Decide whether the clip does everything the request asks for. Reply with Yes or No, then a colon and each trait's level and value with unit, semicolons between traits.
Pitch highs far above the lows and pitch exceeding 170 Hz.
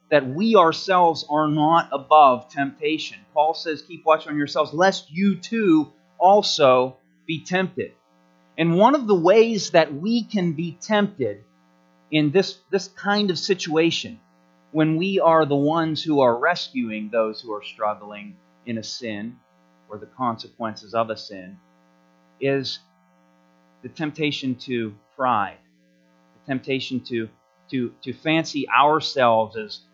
No: wide, 8.4 semitones; medium, 140 Hz